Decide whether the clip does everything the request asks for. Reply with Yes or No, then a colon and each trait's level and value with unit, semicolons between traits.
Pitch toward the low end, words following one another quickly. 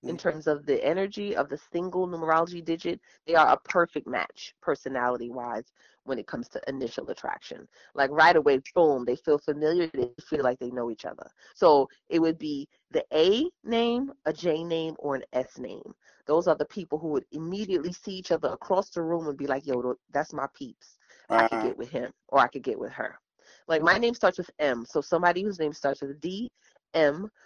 No: medium, 160 Hz; fast, 210 wpm